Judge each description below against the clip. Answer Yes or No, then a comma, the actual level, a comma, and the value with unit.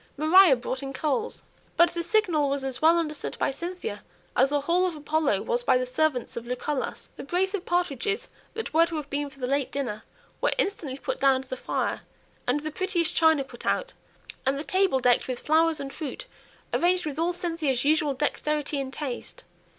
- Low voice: No, very high, 300 Hz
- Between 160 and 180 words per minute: No, average, 200 wpm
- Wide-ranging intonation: No, average, 4.2 semitones